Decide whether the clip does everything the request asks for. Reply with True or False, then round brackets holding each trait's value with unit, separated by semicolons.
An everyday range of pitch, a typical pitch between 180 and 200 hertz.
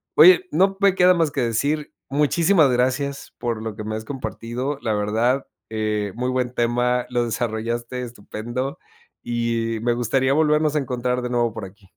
False (3.5 semitones; 125 Hz)